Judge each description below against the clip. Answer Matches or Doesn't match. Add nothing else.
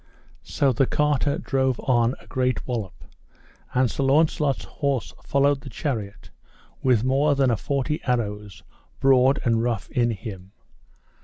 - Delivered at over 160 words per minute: Doesn't match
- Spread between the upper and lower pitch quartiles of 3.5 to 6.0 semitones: Doesn't match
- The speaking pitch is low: Matches